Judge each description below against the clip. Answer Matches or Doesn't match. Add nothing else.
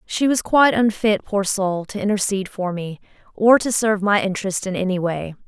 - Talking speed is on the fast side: Doesn't match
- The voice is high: Matches